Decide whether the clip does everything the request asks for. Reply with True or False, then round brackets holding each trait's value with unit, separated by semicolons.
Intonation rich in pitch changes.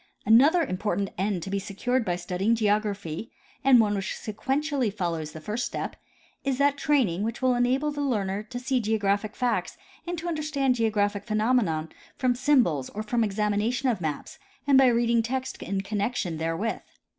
False (4.4 semitones)